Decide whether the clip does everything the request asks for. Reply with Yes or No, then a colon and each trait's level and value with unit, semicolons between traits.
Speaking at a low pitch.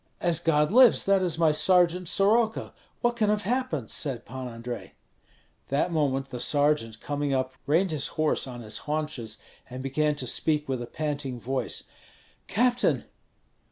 No: medium, 150 Hz